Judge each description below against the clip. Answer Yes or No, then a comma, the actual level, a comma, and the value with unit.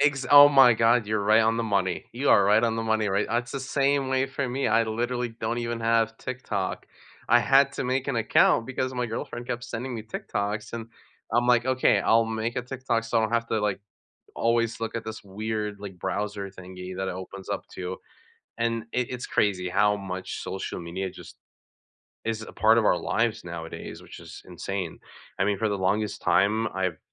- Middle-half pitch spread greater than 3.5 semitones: No, average, 3.0 semitones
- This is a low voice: Yes, low, 115 Hz